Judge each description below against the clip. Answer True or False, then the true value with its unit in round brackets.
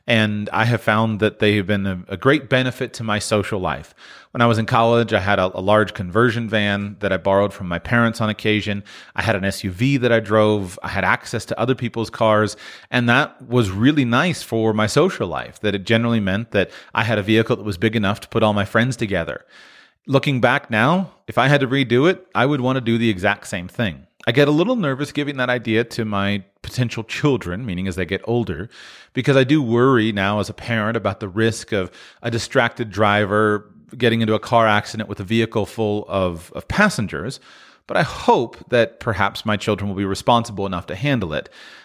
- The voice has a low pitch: True (110 Hz)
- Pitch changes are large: False (2.8 semitones)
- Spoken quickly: True (220 wpm)